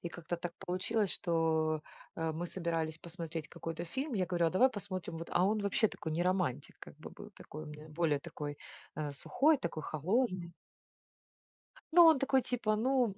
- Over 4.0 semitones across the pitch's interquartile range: Yes, average, 4.7 semitones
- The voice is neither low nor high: Yes, medium, 175 Hz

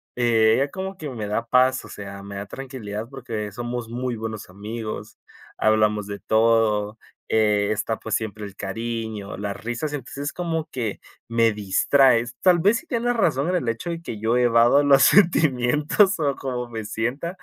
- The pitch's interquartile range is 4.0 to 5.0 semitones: Yes, average, 4.4 semitones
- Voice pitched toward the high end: No, low, 115 Hz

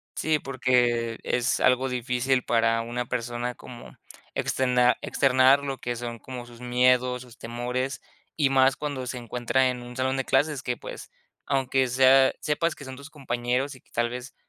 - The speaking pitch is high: No, low, 125 Hz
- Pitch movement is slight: Yes, narrow, 1.6 semitones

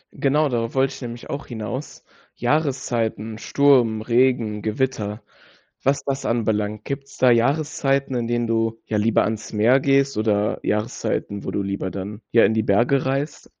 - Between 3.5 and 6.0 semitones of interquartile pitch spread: Yes, average, 4.0 semitones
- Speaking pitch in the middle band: No, low, 120 Hz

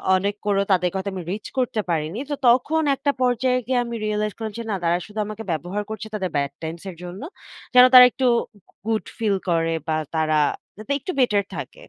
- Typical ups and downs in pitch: Yes, average, 5.0 semitones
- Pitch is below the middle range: No, high, 210 Hz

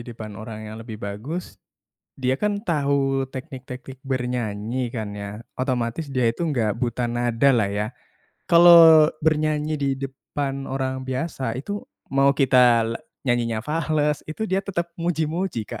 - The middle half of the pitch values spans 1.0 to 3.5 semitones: No, average, 4.3 semitones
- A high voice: No, low, 130 Hz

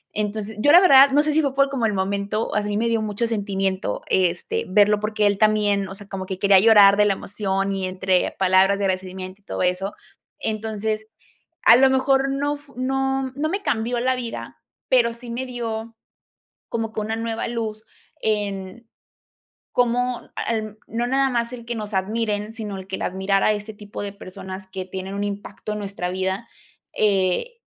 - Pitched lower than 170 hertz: No, high, 215 Hz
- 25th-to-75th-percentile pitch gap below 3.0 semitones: No, average, 3.3 semitones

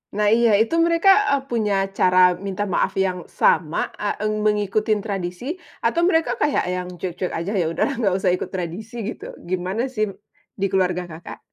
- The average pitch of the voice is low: No, high, 195 Hz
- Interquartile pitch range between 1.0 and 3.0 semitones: No, average, 3.5 semitones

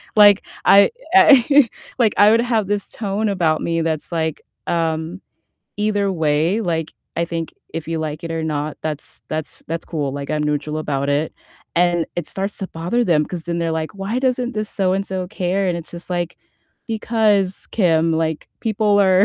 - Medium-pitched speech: Yes, medium, 175 Hz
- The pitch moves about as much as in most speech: Yes, average, 4.2 semitones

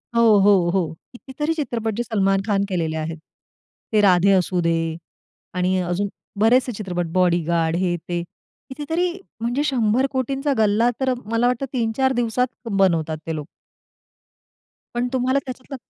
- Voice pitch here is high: Yes, high, 215 Hz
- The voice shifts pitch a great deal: Yes, wide, 5.9 semitones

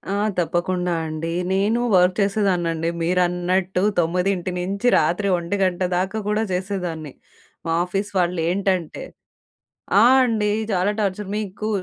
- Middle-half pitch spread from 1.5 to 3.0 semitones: Yes, narrow, 2.4 semitones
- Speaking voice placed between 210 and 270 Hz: No, medium, 185 Hz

